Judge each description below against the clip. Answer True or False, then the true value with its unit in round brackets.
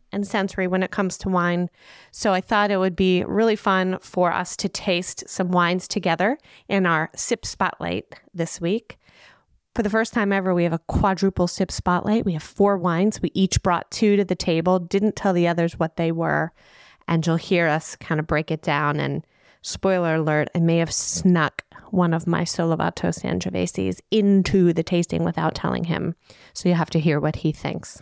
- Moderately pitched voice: True (180 Hz)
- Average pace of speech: True (195 wpm)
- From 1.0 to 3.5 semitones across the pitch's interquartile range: True (2.9 semitones)